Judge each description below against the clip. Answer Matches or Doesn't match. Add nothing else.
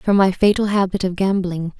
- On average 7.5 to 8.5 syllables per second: Doesn't match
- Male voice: Doesn't match